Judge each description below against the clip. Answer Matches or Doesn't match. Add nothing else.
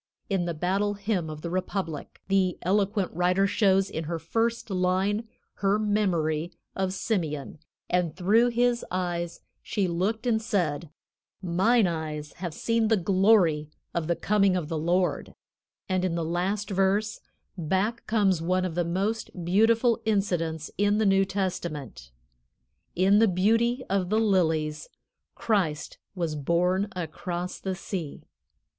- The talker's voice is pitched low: Doesn't match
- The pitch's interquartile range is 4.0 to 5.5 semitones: Doesn't match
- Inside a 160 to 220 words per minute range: Doesn't match